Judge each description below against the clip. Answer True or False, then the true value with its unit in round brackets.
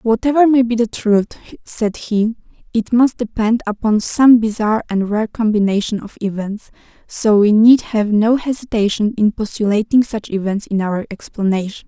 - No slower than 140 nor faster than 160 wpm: True (155 wpm)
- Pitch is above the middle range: True (220 Hz)